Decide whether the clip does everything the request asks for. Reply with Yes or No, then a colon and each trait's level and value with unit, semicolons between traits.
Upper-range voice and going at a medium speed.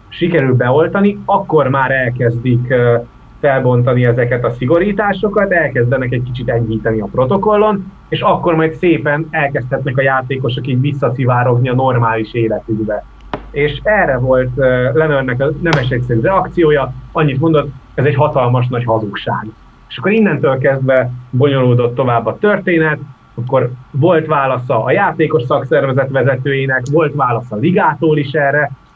No: low, 135 Hz; average, 135 wpm